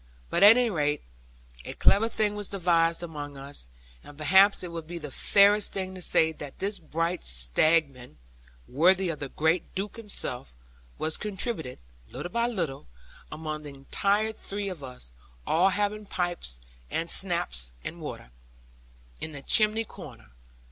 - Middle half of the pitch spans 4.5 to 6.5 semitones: Yes, average, 5.3 semitones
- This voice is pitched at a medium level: Yes, medium, 170 Hz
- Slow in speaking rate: No, average, 155 wpm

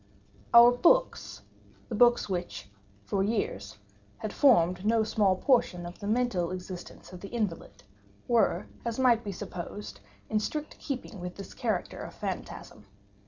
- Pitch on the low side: No, high, 205 Hz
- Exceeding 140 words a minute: No, slow, 135 wpm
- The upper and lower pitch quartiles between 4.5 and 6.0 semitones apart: Yes, average, 5.0 semitones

